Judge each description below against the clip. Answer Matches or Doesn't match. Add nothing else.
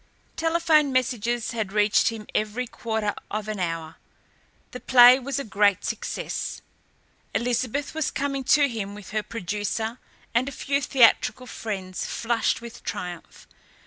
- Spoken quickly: Doesn't match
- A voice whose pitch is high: Matches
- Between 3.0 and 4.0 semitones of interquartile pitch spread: Matches